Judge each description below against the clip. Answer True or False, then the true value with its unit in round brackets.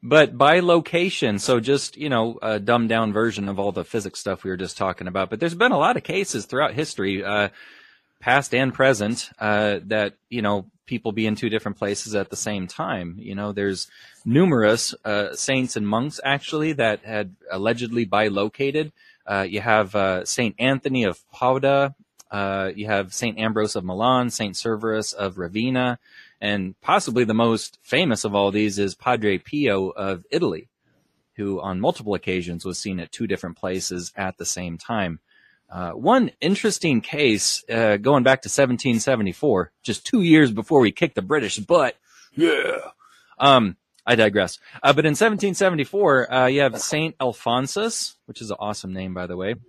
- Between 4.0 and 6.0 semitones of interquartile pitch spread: True (5.0 semitones)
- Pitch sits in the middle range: False (110 Hz)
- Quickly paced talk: False (175 wpm)